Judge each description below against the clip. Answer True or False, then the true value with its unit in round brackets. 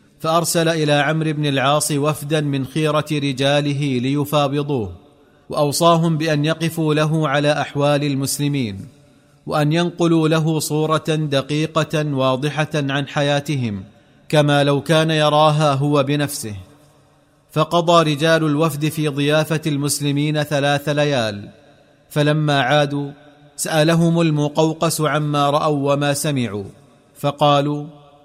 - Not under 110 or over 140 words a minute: False (100 wpm)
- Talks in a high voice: False (145 Hz)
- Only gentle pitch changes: True (1.4 semitones)